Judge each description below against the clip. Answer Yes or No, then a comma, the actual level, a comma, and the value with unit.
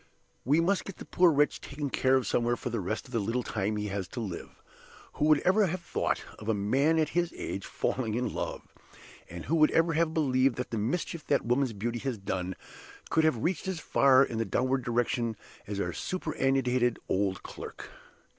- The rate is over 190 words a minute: Yes, fast, 205 wpm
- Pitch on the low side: Yes, low, 130 Hz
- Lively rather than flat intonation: Yes, wide, 5.7 semitones